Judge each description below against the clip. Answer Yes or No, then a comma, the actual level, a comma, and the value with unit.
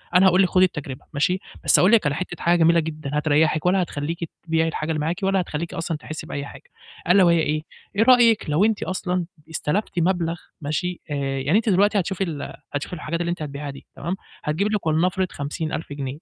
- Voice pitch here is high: No, medium, 165 Hz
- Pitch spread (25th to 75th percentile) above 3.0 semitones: Yes, average, 3.4 semitones